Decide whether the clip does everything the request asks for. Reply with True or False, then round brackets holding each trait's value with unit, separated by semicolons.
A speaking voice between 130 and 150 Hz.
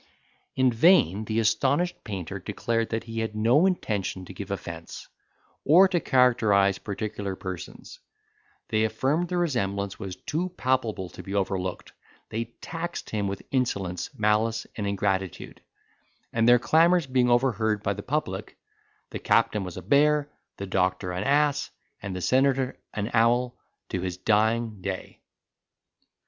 False (110 Hz)